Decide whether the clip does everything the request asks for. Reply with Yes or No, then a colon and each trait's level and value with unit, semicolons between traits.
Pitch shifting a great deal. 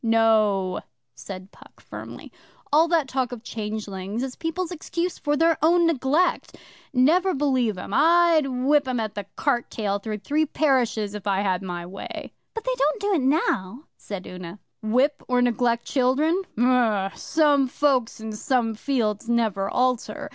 Yes: wide, 5.9 semitones